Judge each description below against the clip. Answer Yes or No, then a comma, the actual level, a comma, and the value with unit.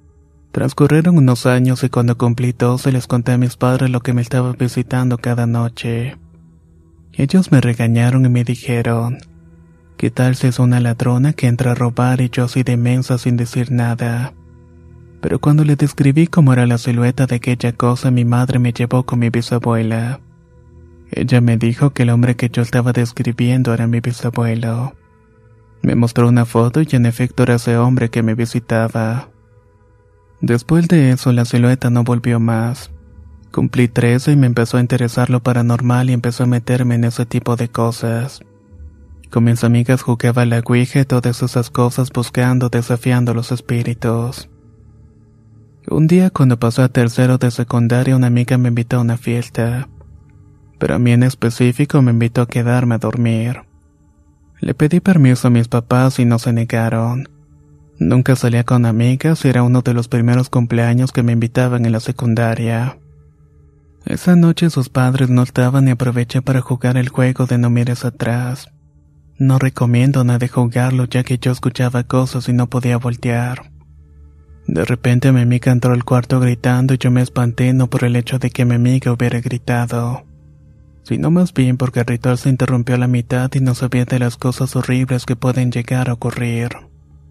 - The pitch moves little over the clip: Yes, narrow, 1.5 semitones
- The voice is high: No, low, 120 Hz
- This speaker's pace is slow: No, average, 175 wpm